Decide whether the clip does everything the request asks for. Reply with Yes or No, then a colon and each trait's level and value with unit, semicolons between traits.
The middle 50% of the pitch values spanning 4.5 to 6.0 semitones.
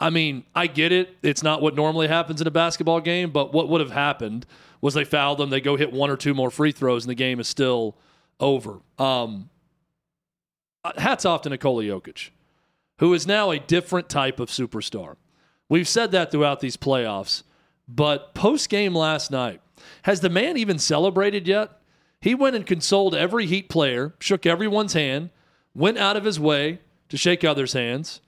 No: average, 3.8 semitones